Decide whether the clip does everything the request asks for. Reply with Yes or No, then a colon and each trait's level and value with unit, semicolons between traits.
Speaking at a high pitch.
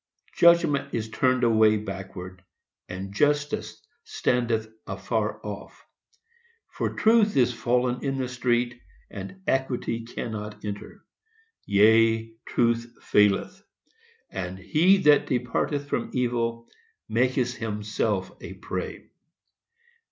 No: low, 115 Hz